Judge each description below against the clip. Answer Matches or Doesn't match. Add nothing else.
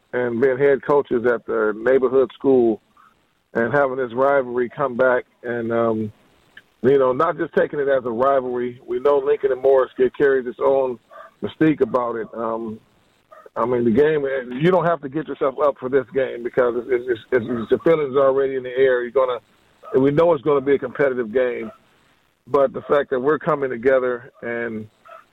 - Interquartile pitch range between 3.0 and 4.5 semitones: Matches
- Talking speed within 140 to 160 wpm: Doesn't match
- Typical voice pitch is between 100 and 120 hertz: Doesn't match